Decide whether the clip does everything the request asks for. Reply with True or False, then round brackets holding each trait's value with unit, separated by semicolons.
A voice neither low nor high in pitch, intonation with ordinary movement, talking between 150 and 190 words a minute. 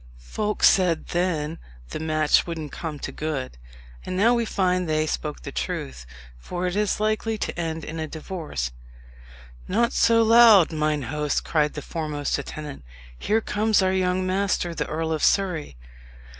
True (165 Hz; 4.2 semitones; 160 wpm)